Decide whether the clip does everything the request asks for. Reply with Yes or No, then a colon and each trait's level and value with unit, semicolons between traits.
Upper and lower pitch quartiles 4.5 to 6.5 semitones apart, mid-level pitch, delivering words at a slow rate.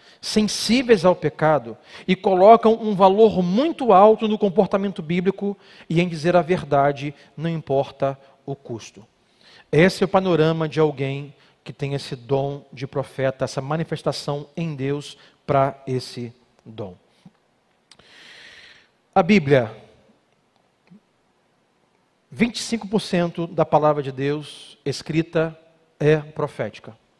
Yes: wide, 5.6 semitones; medium, 155 Hz; slow, 110 wpm